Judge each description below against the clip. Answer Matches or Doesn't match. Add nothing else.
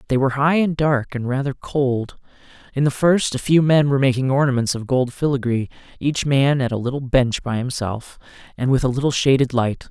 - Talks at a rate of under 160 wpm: Doesn't match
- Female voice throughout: Doesn't match